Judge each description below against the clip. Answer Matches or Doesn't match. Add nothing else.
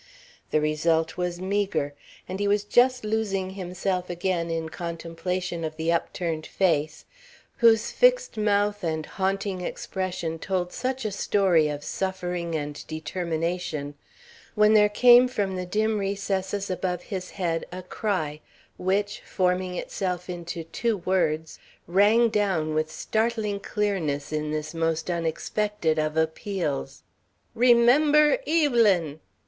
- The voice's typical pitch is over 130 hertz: Matches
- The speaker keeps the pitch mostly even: Doesn't match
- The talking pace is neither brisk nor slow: Doesn't match